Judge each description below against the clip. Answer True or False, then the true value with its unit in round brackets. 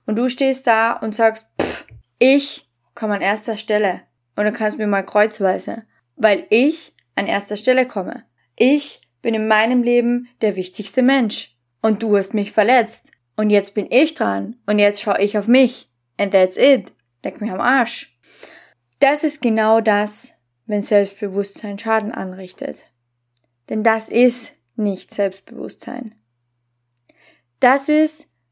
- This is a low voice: False (215 Hz)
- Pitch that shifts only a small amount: False (3.6 semitones)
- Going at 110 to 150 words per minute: True (145 wpm)